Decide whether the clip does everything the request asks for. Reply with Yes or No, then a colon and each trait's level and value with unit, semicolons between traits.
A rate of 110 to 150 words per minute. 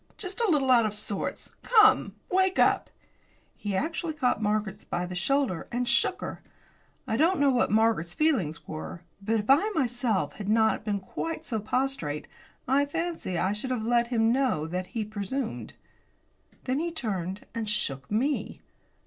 No: average, 170 wpm